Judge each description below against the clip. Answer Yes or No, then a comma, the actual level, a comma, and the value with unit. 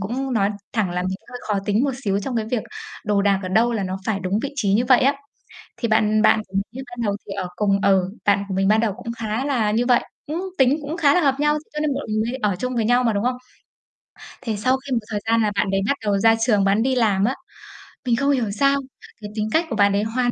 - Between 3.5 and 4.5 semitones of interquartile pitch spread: Yes, average, 4.0 semitones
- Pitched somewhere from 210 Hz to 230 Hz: Yes, high, 220 Hz